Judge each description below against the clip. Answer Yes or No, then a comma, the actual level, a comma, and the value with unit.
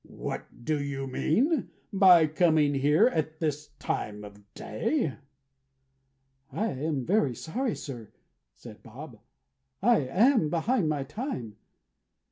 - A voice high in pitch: No, medium, 155 Hz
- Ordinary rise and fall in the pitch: No, wide, 7.0 semitones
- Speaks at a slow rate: Yes, slow, 115 wpm